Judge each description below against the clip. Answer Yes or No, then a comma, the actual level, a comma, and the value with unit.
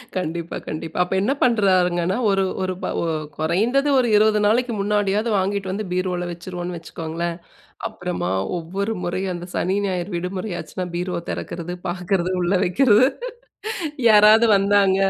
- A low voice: No, medium, 185 Hz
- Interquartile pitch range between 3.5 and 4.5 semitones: No, average, 2.9 semitones